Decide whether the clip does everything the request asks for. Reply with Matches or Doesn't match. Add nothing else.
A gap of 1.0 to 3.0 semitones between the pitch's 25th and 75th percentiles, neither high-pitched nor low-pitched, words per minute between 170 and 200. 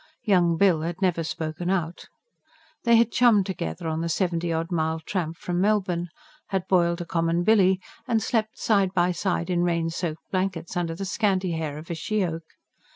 Matches